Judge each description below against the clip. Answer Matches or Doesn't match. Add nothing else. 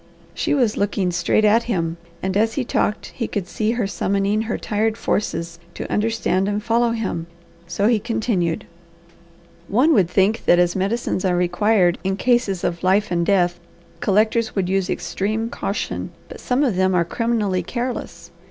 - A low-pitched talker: Doesn't match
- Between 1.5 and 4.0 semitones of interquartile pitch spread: Matches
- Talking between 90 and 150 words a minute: Doesn't match